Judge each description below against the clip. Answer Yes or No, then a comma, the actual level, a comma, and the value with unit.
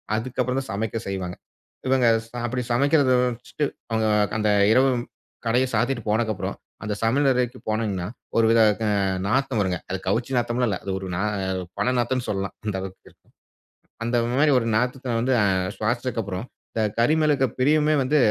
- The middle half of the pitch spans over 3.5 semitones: No, average, 3.1 semitones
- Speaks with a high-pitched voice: No, low, 120 Hz